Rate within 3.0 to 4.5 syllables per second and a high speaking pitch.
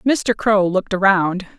Yes: 4.4 syllables/s; high, 200 Hz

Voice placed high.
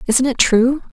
Yes: very high, 255 Hz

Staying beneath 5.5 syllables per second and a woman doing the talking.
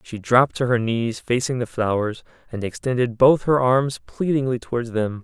No: 5.0 syllables/s; male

